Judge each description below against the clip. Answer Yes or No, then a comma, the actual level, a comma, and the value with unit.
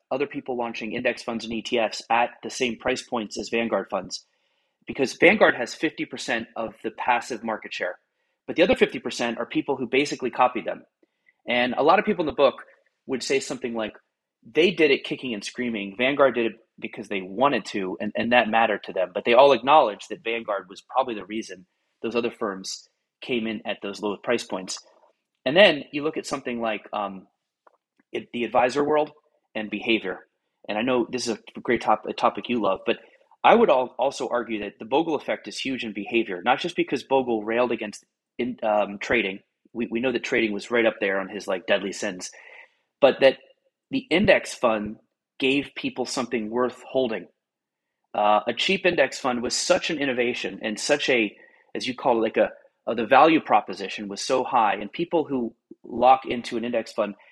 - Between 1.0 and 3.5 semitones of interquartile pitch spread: Yes, average, 3.0 semitones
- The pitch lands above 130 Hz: No, low, 120 Hz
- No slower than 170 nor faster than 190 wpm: No, average, 200 wpm